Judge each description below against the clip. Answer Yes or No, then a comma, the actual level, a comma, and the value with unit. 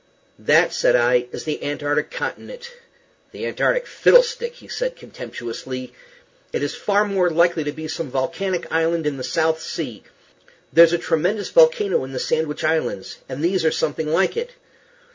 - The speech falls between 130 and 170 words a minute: Yes, average, 160 wpm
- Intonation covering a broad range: Yes, wide, 5.9 semitones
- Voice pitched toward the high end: No, medium, 165 Hz